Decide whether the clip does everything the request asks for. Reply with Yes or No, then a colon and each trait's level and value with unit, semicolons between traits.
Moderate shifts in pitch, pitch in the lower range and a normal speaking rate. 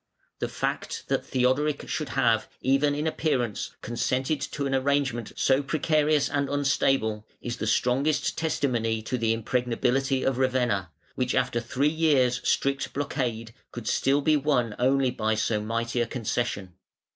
Yes: average, 3.3 semitones; low, 130 Hz; average, 145 wpm